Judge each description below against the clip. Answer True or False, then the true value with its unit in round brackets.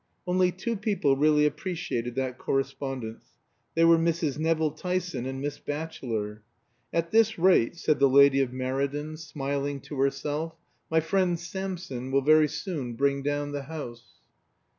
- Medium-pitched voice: True (145 Hz)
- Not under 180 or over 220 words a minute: False (145 wpm)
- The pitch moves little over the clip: False (3.6 semitones)